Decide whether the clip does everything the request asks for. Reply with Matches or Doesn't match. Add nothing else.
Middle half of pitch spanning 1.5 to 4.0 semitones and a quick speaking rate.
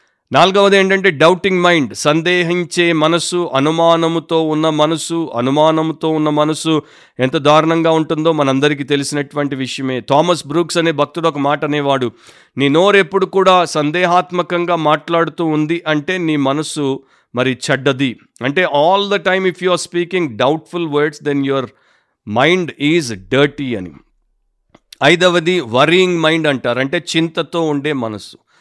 Matches